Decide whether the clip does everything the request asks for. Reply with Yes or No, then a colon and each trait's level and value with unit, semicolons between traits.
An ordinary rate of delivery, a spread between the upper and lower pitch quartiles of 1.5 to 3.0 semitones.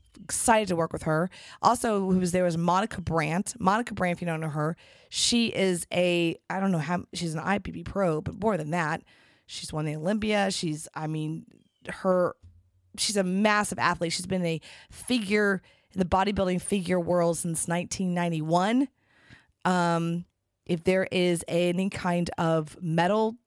Yes: average, 165 wpm; average, 2.7 semitones